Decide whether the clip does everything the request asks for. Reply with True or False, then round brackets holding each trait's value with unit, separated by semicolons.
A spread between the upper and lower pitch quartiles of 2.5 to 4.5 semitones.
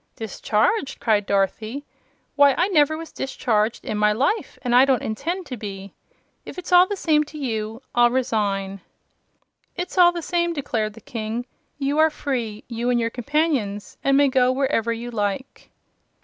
False (5.3 semitones)